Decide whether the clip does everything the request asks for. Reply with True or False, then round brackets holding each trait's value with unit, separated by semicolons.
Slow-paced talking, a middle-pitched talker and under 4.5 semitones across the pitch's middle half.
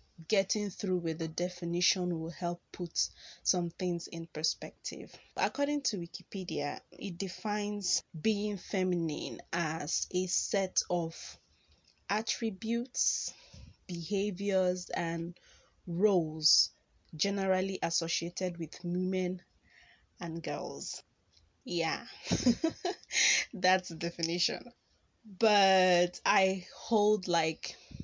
True (90 wpm; 180 Hz; 3.0 semitones)